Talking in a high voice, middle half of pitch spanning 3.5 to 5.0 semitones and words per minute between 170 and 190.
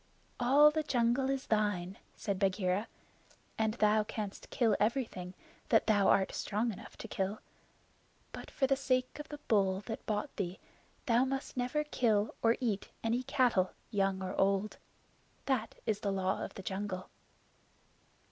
No: high, 215 Hz; average, 4.3 semitones; average, 155 wpm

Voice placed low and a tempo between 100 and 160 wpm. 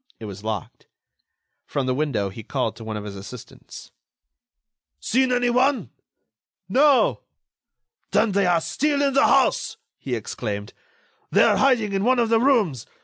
No: medium, 180 Hz; average, 150 wpm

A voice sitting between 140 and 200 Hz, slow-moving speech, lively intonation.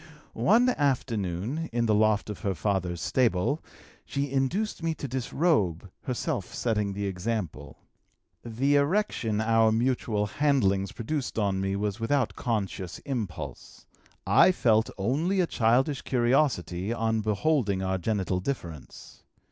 No: low, 110 Hz; slow, 125 wpm; wide, 5.8 semitones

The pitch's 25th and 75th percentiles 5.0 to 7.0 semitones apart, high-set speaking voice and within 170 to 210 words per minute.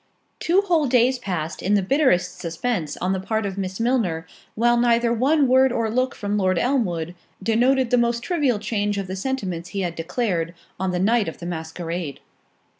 Yes: wide, 5.4 semitones; high, 210 Hz; average, 190 wpm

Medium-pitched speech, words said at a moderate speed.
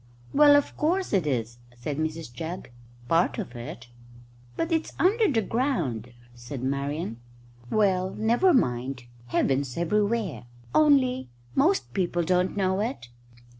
No: medium, 180 Hz; slow, 130 wpm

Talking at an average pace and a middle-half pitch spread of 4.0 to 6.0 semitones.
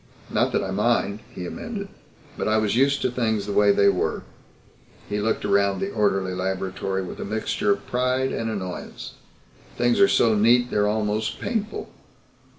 No: average, 170 wpm; average, 3.4 semitones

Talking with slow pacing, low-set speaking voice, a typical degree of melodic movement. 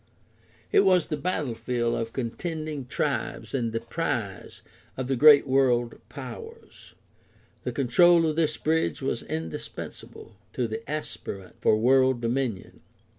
Yes: slow, 125 wpm; low, 130 Hz; average, 4.9 semitones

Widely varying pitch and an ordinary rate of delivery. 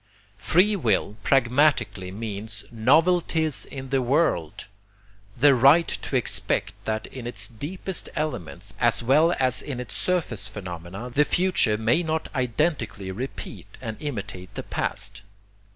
No: wide, 6.3 semitones; slow, 130 wpm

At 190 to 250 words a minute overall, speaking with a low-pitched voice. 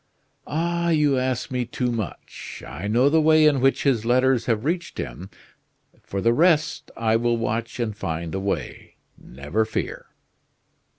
No: average, 160 wpm; low, 120 Hz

